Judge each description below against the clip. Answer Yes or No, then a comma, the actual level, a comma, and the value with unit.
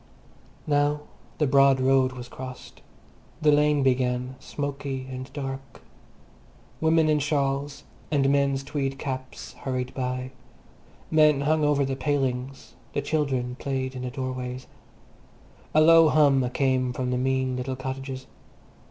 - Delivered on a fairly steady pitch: Yes, narrow, 1.9 semitones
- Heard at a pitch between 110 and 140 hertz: Yes, low, 135 Hz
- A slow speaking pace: Yes, slow, 130 wpm